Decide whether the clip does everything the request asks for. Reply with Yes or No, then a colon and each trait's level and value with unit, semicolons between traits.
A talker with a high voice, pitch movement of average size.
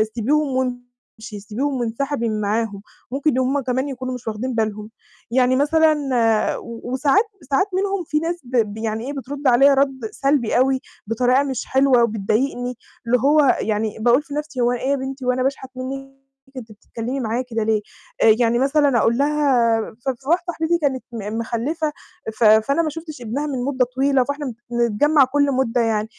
Yes: very high, 255 Hz; average, 3.4 semitones